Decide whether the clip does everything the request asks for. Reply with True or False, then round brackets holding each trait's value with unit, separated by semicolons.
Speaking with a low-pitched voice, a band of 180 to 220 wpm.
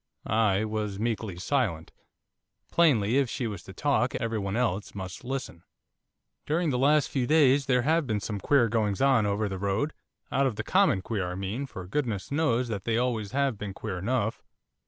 True (115 Hz; 190 wpm)